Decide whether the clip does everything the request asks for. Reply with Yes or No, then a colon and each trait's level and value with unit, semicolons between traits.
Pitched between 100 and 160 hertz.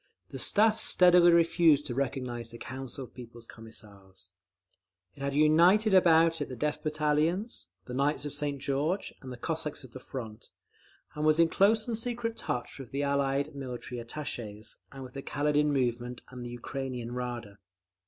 Yes: medium, 140 Hz